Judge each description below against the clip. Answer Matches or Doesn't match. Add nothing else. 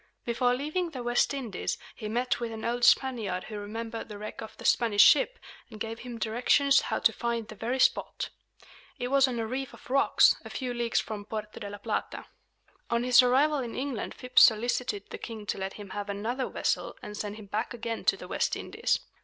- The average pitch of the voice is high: Matches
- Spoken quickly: Matches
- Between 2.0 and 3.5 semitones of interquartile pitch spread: Matches